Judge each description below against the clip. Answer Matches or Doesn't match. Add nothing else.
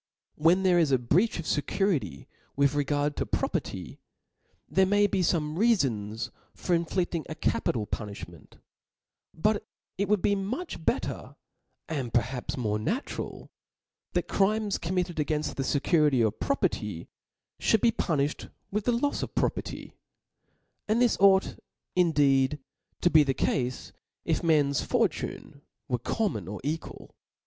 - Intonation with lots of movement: Matches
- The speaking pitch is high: Doesn't match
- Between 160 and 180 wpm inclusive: Doesn't match